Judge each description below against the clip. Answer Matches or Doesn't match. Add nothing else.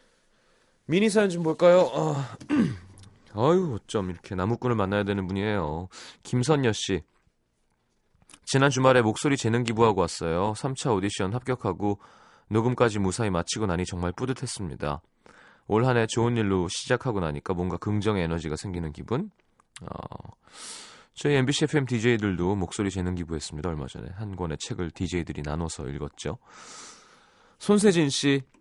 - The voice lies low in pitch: Matches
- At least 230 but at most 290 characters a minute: Doesn't match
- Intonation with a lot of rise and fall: Matches